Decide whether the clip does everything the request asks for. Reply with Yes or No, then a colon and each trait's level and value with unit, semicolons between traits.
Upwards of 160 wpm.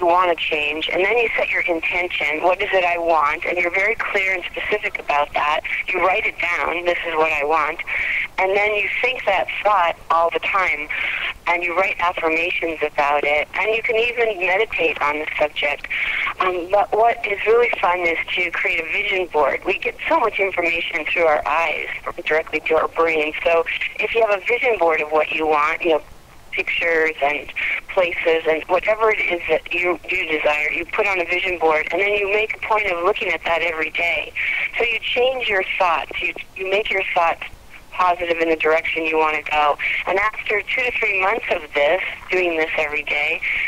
Yes: fast, 205 wpm